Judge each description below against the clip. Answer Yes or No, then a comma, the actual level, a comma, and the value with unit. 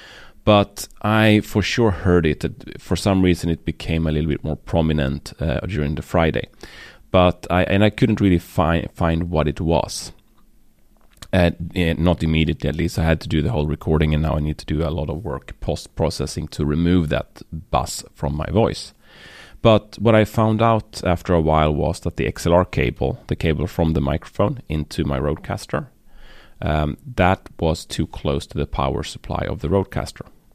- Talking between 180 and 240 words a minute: Yes, average, 190 wpm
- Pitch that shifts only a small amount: No, average, 3.8 semitones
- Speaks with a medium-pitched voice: No, very low, 85 Hz